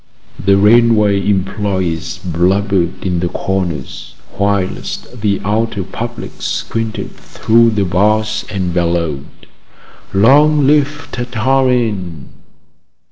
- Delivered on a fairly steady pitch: No, average, 4.0 semitones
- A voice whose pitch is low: Yes, low, 100 Hz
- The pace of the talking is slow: Yes, slow, 90 wpm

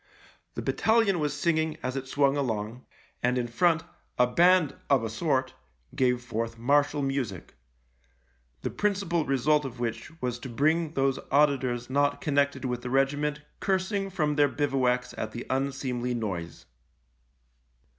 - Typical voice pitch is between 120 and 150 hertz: Yes, low, 135 Hz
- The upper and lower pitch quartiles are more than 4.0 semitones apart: No, average, 3.5 semitones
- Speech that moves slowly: No, average, 145 wpm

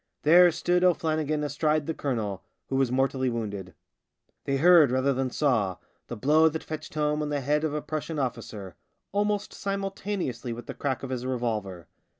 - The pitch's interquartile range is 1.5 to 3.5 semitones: No, average, 4.3 semitones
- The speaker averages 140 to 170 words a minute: No, average, 180 wpm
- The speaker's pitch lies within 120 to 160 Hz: Yes, medium, 140 Hz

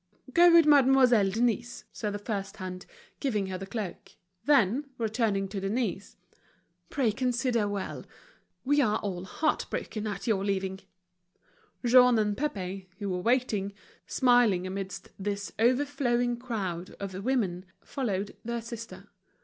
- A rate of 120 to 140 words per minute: Yes, slow, 135 wpm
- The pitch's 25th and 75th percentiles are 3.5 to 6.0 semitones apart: Yes, average, 4.2 semitones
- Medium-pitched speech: No, high, 215 Hz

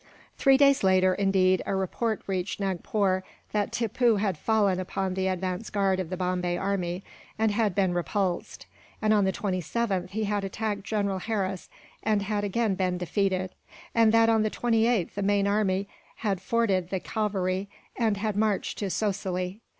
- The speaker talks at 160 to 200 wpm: Yes, average, 165 wpm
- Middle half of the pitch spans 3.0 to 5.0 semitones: No, narrow, 2.5 semitones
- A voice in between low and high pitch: No, high, 195 Hz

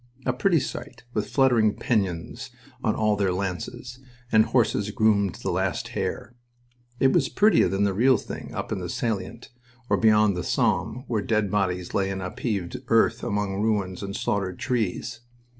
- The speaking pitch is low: Yes, low, 105 Hz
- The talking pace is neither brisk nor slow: Yes, average, 170 wpm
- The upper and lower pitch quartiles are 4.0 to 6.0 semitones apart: No, average, 3.5 semitones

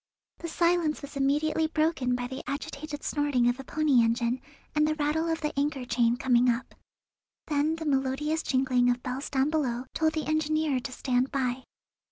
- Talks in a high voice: Yes, very high, 280 Hz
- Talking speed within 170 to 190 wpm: Yes, average, 180 wpm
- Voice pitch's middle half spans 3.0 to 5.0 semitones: Yes, average, 3.6 semitones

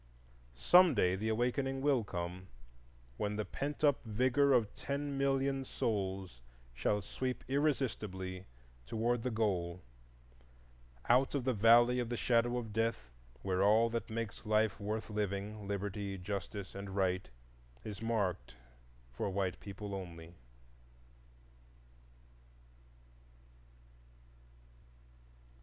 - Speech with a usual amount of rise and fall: Yes, average, 4.3 semitones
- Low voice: Yes, low, 105 Hz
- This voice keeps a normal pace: No, slow, 105 wpm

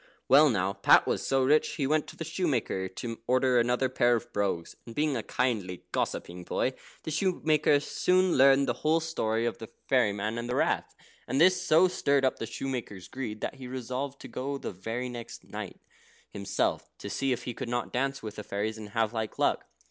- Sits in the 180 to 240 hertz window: No, low, 125 Hz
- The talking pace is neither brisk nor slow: No, fast, 210 wpm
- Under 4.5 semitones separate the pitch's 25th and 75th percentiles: Yes, average, 4.1 semitones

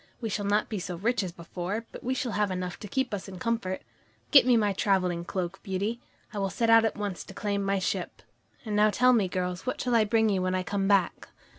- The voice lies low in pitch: No, high, 205 Hz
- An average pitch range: Yes, average, 3.3 semitones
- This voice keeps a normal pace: No, fast, 250 wpm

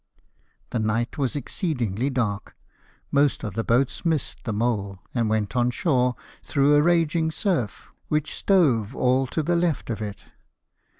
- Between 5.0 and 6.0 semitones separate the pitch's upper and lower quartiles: Yes, average, 5.3 semitones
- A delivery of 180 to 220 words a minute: No, average, 155 wpm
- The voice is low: Yes, low, 125 Hz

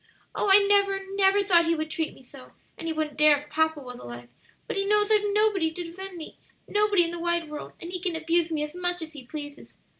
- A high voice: Yes, very high, 335 Hz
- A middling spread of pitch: Yes, average, 4.2 semitones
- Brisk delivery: Yes, fast, 245 wpm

